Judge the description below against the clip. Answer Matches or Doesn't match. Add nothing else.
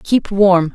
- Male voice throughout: Doesn't match